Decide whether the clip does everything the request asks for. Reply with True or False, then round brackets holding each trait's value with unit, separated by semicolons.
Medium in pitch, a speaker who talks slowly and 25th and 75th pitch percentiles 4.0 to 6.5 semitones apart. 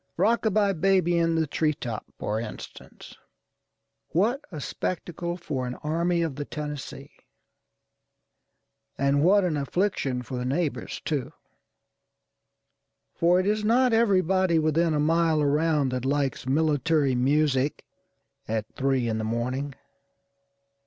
True (155 Hz; 130 wpm; 4.6 semitones)